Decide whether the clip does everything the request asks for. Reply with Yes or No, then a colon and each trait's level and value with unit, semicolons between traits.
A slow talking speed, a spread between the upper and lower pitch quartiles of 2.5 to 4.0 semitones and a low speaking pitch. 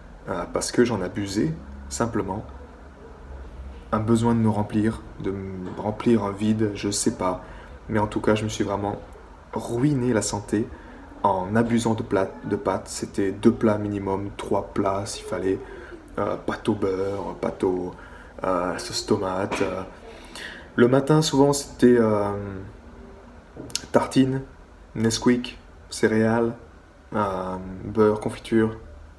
Yes: slow, 135 wpm; average, 3.5 semitones; low, 100 Hz